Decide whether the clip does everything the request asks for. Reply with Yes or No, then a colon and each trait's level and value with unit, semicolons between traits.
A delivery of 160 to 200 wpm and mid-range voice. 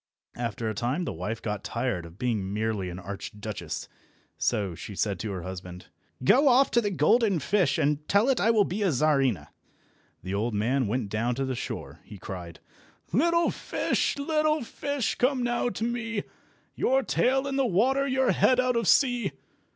Yes: average, 180 wpm; medium, 150 Hz